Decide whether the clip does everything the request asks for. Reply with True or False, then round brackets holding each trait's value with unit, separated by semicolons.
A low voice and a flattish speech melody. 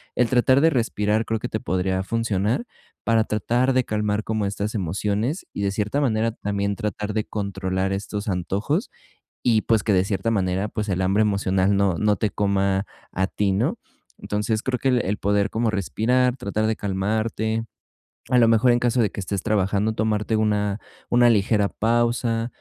True (105 Hz; 2.3 semitones)